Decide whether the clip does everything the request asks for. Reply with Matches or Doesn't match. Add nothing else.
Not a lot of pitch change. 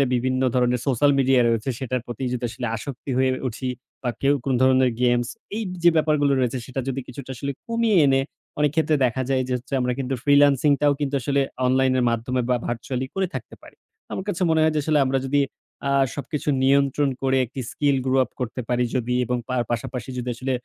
Matches